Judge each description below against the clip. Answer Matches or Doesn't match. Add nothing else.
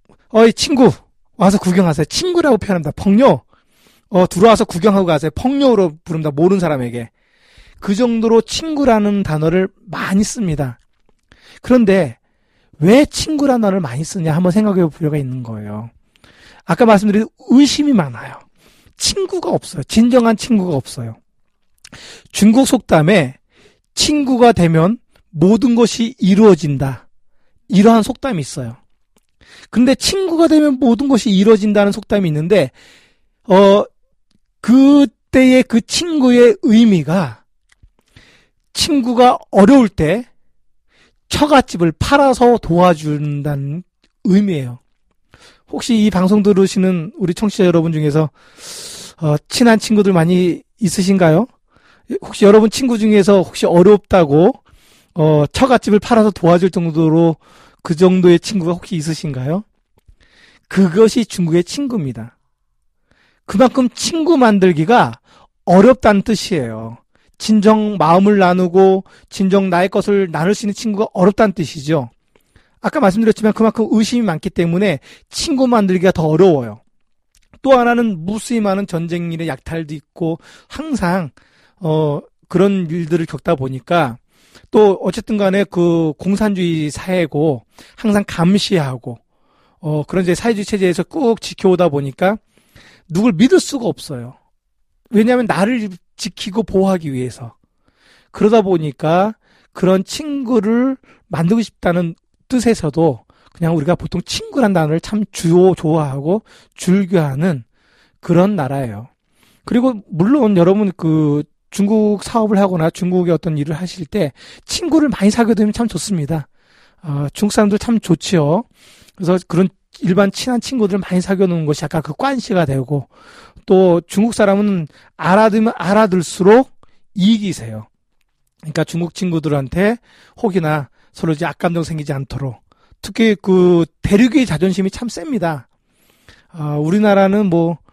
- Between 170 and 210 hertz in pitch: Matches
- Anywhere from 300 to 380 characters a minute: Doesn't match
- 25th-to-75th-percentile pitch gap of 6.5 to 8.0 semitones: Doesn't match